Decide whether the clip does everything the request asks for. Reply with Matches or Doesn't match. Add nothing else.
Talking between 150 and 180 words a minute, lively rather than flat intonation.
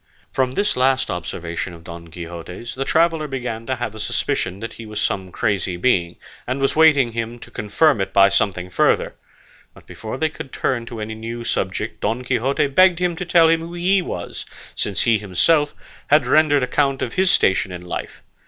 Doesn't match